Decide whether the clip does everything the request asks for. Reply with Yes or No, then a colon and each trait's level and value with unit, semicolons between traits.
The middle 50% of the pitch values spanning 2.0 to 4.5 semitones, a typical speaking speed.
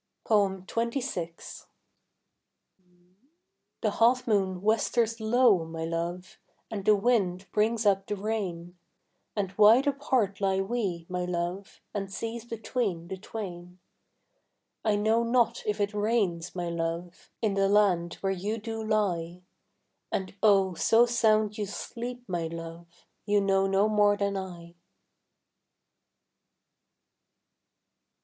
No: average, 3.7 semitones; slow, 120 wpm